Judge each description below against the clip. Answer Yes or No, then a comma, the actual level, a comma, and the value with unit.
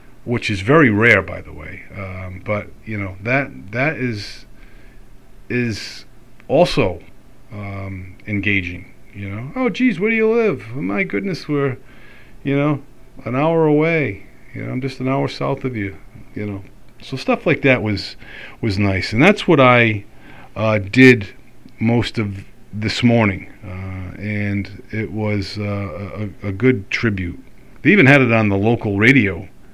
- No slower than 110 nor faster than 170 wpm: Yes, average, 160 wpm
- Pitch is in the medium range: No, low, 110 Hz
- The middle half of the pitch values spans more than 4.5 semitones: Yes, average, 4.9 semitones